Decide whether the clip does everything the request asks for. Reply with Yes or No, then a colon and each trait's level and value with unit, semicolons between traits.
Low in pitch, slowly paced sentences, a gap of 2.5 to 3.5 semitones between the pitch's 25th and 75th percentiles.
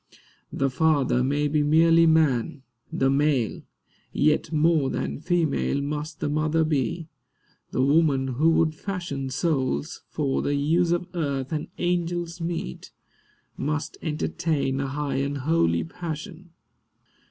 No: medium, 150 Hz; slow, 130 wpm; average, 3.1 semitones